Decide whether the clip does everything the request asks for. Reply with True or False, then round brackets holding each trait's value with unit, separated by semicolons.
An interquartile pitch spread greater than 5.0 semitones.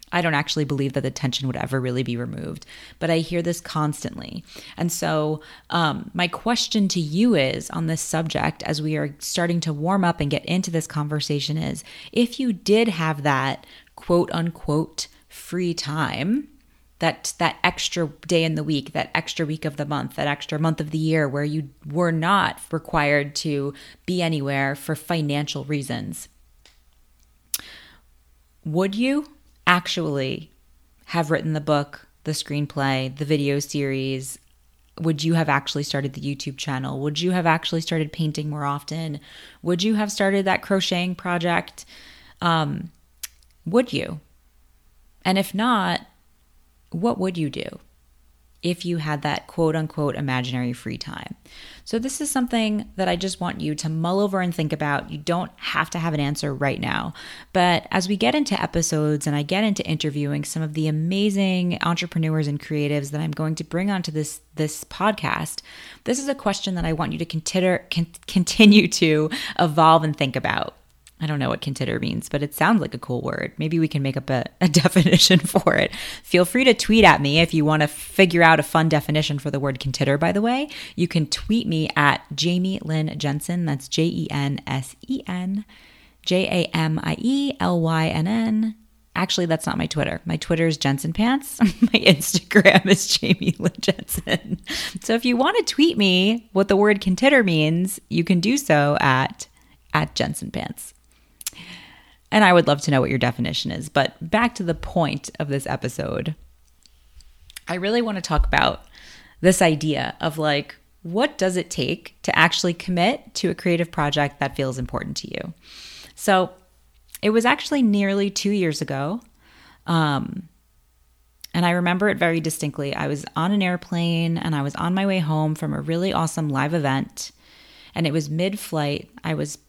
False (4.3 semitones)